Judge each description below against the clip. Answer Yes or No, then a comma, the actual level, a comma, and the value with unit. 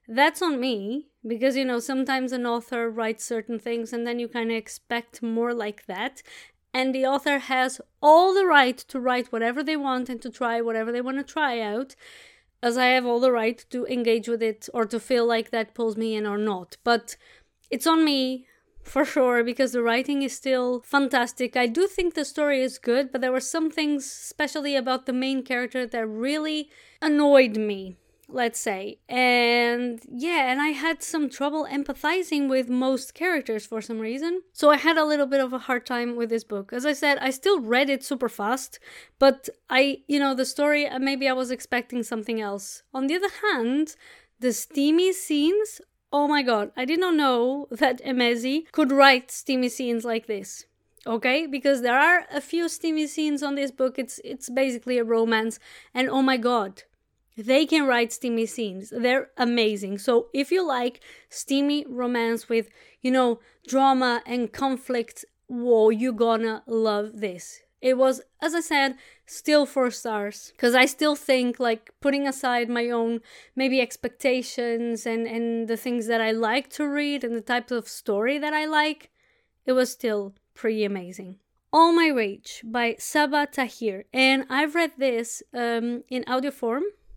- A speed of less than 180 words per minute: No, average, 185 wpm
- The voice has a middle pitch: No, very high, 255 Hz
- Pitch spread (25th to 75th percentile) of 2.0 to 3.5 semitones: Yes, average, 3.2 semitones